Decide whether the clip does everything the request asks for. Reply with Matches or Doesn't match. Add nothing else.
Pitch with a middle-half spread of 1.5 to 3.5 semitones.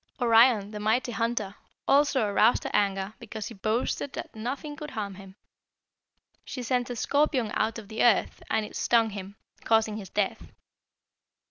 Matches